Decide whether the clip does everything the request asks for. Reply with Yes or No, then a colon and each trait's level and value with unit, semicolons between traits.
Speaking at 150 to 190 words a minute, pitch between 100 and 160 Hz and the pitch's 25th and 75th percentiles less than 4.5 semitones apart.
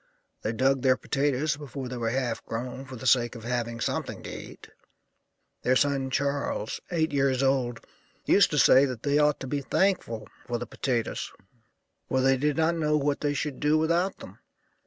Yes: average, 185 wpm; low, 135 Hz; average, 2.8 semitones